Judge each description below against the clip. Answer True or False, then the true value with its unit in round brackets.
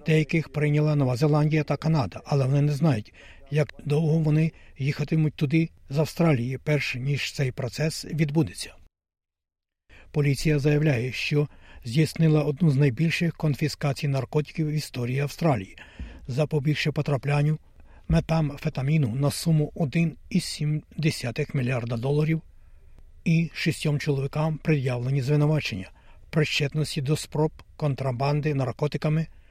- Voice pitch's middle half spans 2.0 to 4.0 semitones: True (2.7 semitones)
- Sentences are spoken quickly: False (110 wpm)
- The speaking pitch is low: False (150 Hz)